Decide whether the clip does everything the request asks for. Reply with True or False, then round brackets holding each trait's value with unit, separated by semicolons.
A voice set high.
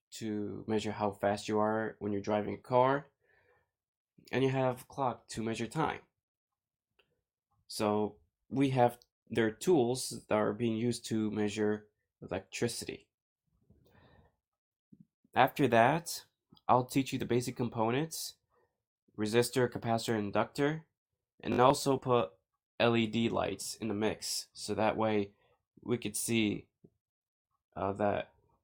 False (115 Hz)